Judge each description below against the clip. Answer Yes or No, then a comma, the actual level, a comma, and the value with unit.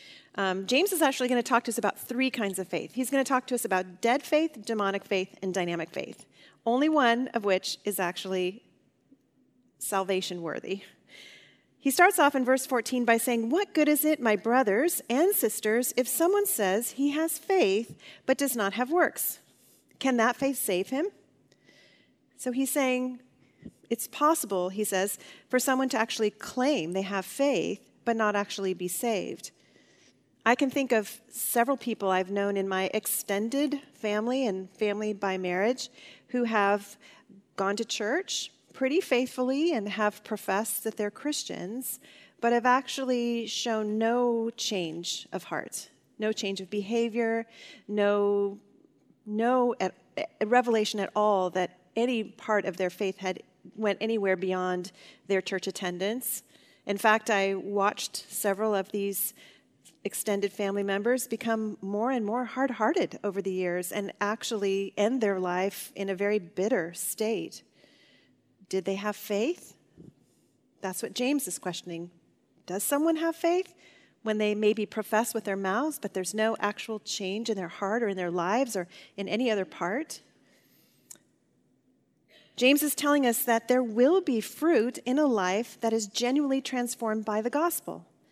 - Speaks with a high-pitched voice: Yes, high, 220 Hz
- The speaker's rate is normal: Yes, average, 160 wpm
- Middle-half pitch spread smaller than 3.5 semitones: No, average, 4.3 semitones